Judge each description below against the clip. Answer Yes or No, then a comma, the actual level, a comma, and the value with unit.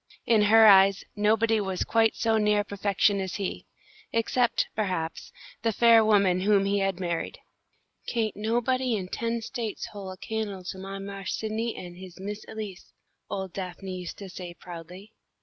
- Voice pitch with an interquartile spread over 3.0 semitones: No, narrow, 2.6 semitones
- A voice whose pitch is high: Yes, high, 205 Hz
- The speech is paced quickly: No, average, 165 wpm